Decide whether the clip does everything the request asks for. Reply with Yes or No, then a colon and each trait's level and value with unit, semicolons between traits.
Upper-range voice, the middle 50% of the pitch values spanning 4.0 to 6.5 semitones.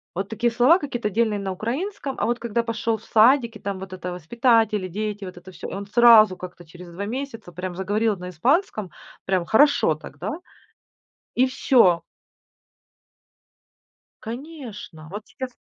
Yes: high, 215 Hz; average, 4.4 semitones